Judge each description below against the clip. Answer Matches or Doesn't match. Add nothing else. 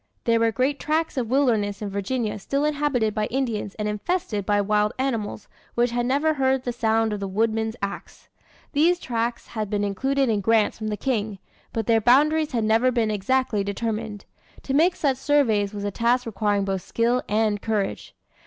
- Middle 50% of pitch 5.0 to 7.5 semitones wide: Doesn't match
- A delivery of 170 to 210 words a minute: Matches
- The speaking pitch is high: Matches